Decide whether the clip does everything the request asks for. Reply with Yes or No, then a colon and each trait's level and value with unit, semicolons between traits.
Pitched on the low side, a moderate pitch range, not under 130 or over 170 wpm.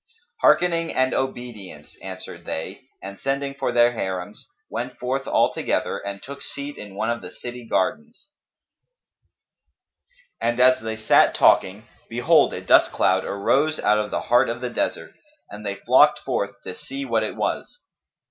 Yes: low, 120 Hz; average, 4.8 semitones; average, 160 wpm